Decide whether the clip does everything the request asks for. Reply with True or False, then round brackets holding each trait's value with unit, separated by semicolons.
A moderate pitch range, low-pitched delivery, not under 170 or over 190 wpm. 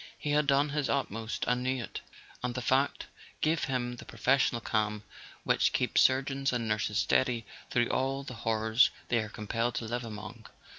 True (3.2 semitones; 120 Hz; 185 wpm)